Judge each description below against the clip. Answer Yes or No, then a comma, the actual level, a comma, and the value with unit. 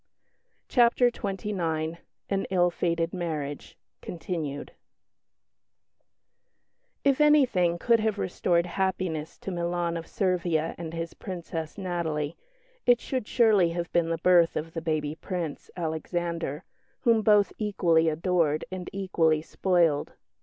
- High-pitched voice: No, medium, 175 Hz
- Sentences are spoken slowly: Yes, slow, 120 wpm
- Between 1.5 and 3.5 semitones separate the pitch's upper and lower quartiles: Yes, average, 2.9 semitones